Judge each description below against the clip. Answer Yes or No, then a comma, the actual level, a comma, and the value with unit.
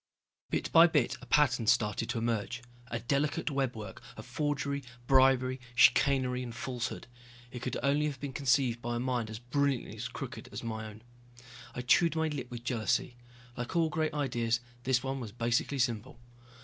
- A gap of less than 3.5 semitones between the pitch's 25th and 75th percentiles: Yes, average, 2.9 semitones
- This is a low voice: Yes, low, 125 Hz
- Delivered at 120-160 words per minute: No, average, 170 wpm